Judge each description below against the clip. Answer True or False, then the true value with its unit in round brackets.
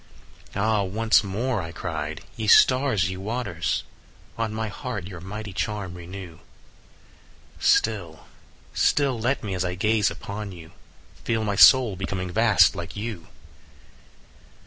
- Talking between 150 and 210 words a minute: False (135 wpm)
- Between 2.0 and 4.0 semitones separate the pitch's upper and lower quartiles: True (3.4 semitones)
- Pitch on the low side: True (100 Hz)